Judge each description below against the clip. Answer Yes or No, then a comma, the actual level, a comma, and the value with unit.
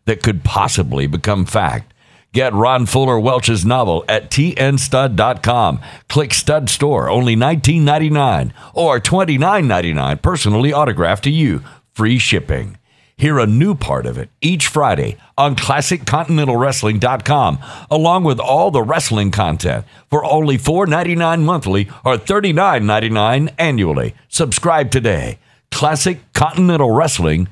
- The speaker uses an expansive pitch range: Yes, wide, 5.7 semitones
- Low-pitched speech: Yes, low, 130 Hz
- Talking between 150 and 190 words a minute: No, average, 140 wpm